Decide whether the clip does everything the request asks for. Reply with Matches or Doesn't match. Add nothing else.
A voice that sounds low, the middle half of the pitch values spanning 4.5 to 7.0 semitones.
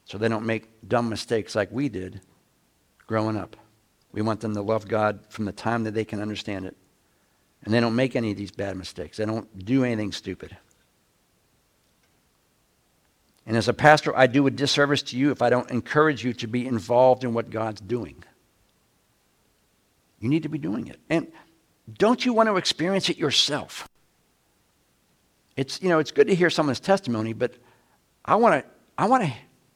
Matches